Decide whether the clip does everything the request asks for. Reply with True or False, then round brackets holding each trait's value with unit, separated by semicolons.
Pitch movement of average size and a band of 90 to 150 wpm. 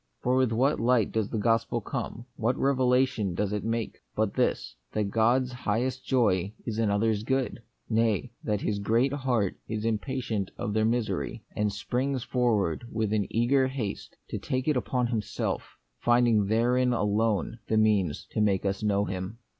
False (3.0 semitones; 170 wpm)